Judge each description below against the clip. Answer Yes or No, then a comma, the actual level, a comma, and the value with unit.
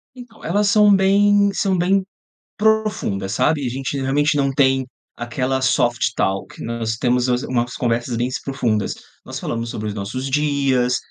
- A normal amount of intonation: No, wide, 7.2 semitones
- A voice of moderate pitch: No, low, 130 Hz